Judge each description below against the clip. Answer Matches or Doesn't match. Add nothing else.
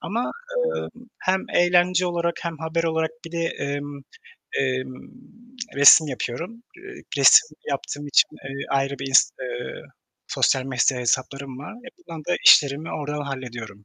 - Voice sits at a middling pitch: Matches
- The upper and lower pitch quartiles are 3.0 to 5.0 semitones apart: Matches